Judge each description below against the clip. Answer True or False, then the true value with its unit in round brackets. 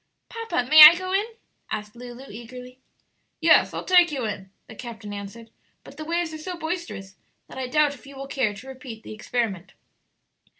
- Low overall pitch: False (255 Hz)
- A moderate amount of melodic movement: False (5.8 semitones)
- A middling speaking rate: True (185 wpm)